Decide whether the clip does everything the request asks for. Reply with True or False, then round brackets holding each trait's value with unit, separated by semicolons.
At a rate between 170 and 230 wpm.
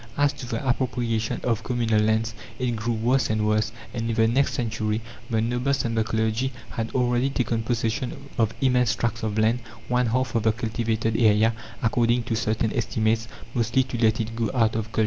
True (195 wpm)